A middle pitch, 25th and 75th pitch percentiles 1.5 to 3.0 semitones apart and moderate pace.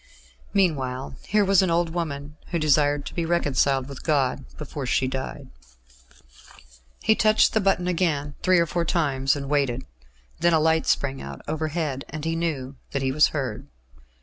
No: medium, 150 Hz; average, 3.9 semitones; average, 170 wpm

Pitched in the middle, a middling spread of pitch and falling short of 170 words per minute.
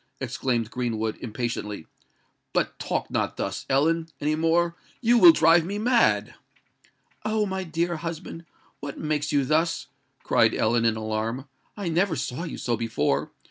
No: medium, 155 Hz; wide, 6.4 semitones; average, 145 wpm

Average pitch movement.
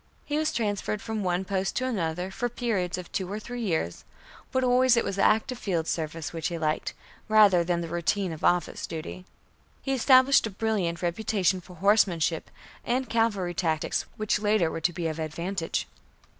Yes: average, 4.6 semitones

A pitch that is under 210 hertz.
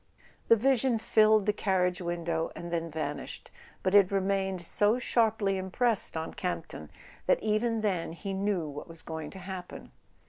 Yes: high, 190 Hz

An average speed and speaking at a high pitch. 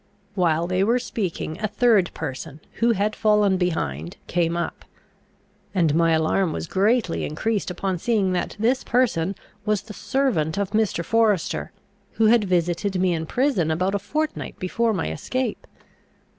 Yes: average, 155 wpm; high, 195 Hz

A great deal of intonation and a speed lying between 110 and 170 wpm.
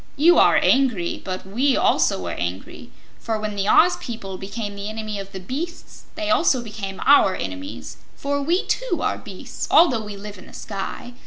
No: wide, 6.1 semitones; average, 185 wpm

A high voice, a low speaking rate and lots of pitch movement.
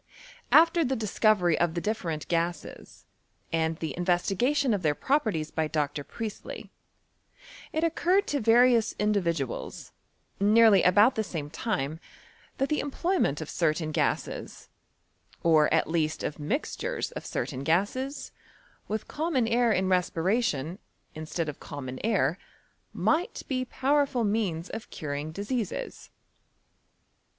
Yes: high, 195 Hz; slow, 125 wpm; wide, 7.4 semitones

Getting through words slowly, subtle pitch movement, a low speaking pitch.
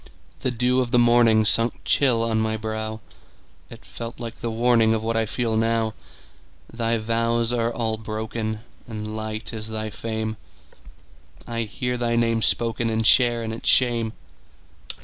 Yes: slow, 130 wpm; narrow, 1.2 semitones; low, 115 Hz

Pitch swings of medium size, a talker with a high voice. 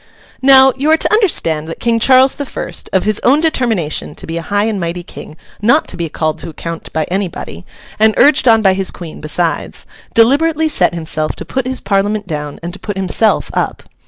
No: wide, 7.7 semitones; high, 205 Hz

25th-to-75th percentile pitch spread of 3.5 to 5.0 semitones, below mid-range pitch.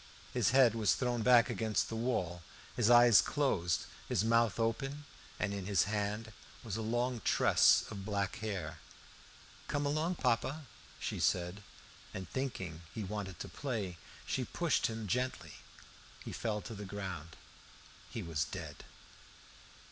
Yes: average, 4.0 semitones; low, 110 Hz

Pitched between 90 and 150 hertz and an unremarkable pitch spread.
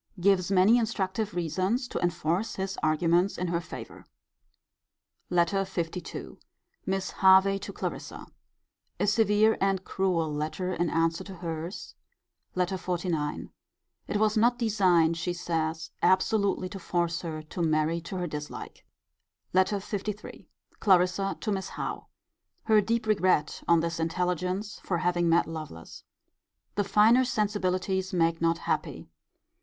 No: medium, 185 Hz; average, 3.0 semitones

